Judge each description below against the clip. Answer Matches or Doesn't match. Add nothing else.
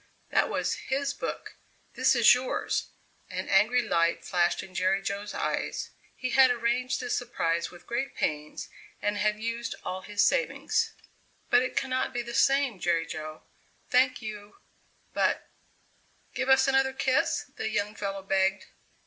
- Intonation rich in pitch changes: Doesn't match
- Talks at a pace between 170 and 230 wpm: Doesn't match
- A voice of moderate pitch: Doesn't match